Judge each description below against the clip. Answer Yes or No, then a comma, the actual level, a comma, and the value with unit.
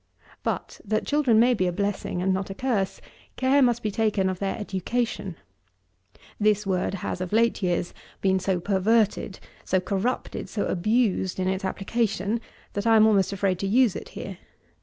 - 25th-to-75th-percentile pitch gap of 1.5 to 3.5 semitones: Yes, average, 3.1 semitones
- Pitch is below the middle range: No, high, 200 Hz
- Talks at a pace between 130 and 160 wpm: No, average, 175 wpm